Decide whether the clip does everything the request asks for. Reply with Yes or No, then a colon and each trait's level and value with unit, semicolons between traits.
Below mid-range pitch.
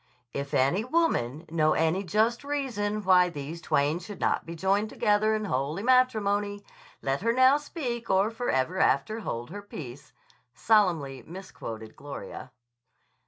No: high, 195 Hz